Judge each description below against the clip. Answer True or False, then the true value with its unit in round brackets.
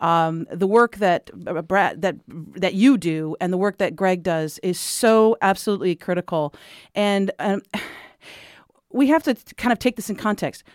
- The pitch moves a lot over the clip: False (3.9 semitones)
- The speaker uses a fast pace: False (175 wpm)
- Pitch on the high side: True (195 Hz)